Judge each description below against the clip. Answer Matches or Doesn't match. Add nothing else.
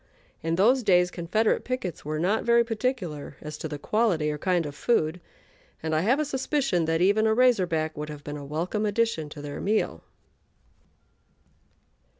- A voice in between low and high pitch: Matches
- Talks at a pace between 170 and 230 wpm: Matches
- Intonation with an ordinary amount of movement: Doesn't match